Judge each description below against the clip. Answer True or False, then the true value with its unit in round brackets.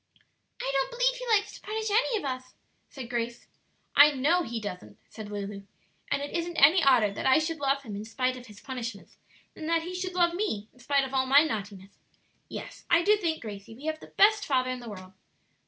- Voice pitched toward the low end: False (270 Hz)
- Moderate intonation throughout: False (6.9 semitones)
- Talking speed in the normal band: False (220 wpm)